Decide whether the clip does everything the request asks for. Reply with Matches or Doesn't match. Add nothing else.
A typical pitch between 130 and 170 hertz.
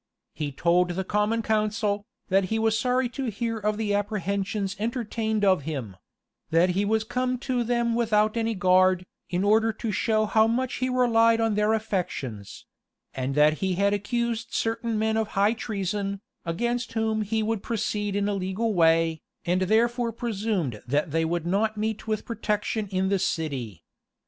Doesn't match